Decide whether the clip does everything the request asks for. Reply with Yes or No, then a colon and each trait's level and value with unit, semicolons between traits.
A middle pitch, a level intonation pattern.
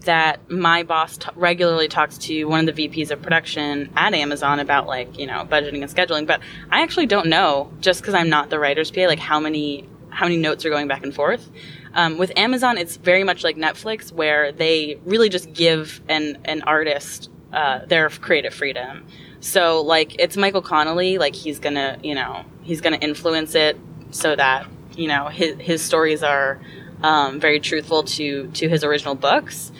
Yes: medium, 155 Hz; narrow, 2.2 semitones